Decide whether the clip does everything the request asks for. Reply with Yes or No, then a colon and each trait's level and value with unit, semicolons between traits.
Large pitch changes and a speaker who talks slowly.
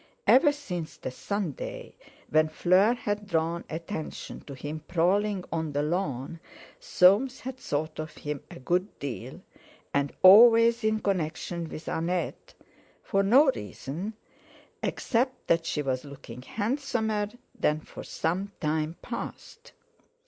Yes: wide, 5.9 semitones; slow, 125 wpm